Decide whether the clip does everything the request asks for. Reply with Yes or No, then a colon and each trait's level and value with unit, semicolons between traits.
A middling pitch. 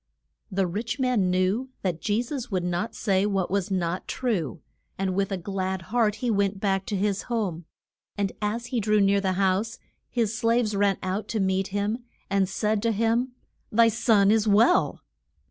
No: high, 200 Hz